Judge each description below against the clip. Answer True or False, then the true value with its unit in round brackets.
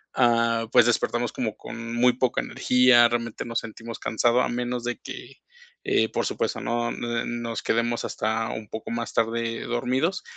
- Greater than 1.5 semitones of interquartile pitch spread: False (0.9 semitones)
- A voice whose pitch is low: True (120 Hz)